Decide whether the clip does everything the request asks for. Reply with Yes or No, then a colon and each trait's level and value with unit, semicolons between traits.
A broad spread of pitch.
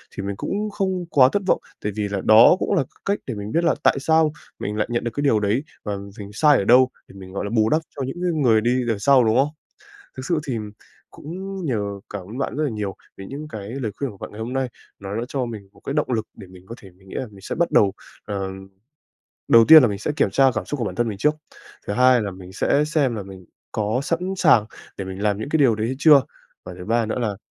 Yes: wide, 5.8 semitones